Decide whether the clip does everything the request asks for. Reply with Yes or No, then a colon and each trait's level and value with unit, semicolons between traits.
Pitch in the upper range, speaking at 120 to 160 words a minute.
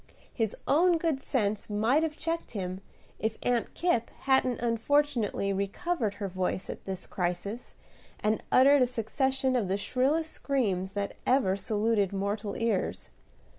Yes: high, 225 Hz; average, 140 wpm